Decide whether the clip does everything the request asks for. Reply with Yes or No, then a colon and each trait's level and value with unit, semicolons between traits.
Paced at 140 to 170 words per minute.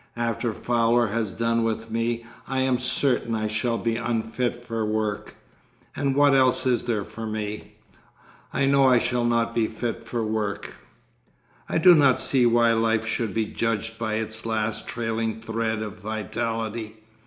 Yes: average, 160 wpm